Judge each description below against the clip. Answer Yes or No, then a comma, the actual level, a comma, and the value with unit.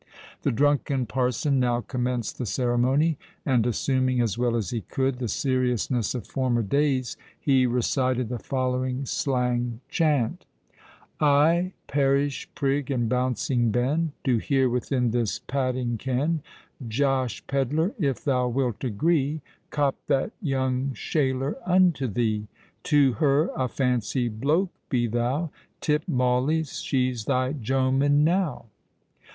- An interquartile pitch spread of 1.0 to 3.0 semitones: Yes, narrow, 2.6 semitones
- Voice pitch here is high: No, low, 130 Hz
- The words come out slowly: Yes, slow, 125 wpm